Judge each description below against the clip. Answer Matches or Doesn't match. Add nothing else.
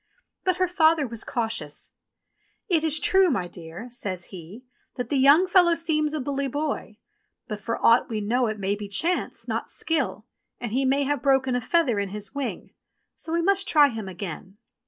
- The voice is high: Matches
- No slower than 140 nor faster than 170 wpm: Doesn't match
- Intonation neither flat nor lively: Doesn't match